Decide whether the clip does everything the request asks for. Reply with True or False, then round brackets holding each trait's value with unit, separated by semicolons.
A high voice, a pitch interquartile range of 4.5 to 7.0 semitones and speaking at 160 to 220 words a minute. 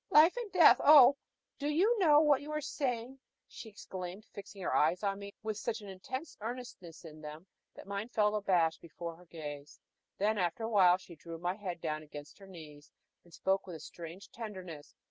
True (195 Hz; 5.6 semitones; 190 wpm)